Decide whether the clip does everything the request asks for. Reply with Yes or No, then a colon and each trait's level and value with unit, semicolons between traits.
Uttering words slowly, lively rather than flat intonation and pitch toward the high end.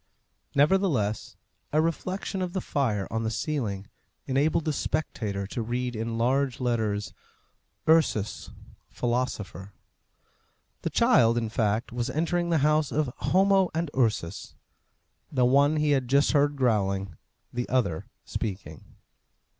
No: slow, 125 wpm; wide, 5.8 semitones; low, 125 Hz